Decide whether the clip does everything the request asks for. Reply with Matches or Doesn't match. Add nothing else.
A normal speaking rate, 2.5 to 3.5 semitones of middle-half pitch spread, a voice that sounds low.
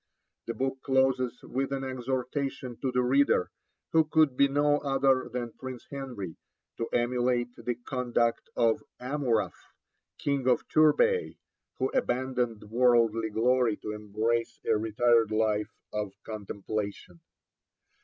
Doesn't match